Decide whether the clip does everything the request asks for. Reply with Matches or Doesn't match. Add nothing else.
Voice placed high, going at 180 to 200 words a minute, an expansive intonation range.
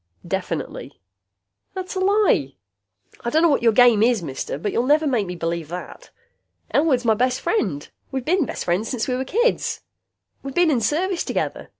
Matches